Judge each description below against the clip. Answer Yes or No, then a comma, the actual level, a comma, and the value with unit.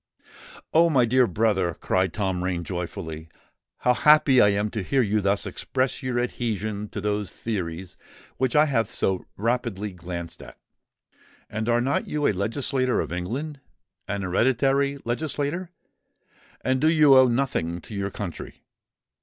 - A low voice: Yes, low, 110 Hz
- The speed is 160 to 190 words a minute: No, average, 145 wpm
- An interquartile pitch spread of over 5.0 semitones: Yes, wide, 5.4 semitones